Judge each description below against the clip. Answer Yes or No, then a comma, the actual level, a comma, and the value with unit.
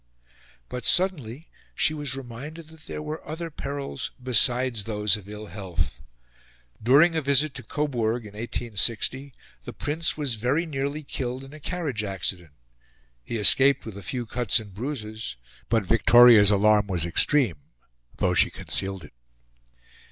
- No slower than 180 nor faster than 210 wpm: No, average, 145 wpm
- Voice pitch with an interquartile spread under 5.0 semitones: No, wide, 5.4 semitones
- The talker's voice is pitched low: Yes, low, 125 Hz